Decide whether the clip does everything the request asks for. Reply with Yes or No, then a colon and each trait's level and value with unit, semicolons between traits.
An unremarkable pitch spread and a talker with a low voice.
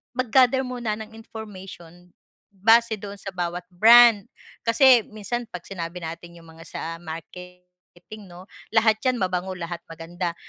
No: average, 4.2 semitones; high, 190 Hz